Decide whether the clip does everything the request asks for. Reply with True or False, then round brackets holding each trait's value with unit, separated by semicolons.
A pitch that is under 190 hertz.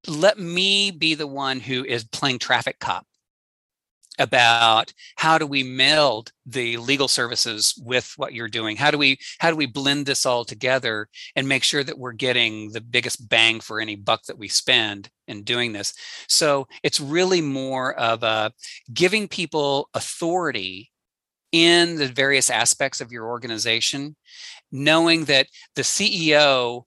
True (135 Hz)